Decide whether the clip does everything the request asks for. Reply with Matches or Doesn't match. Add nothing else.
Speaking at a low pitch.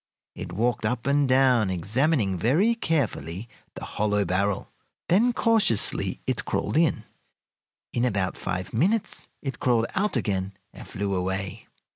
Matches